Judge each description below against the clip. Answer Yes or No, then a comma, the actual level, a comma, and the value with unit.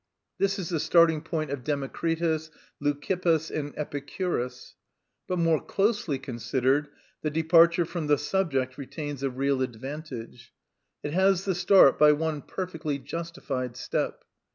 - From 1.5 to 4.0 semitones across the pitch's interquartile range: Yes, average, 3.6 semitones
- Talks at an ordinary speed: No, slow, 130 wpm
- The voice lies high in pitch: No, medium, 150 Hz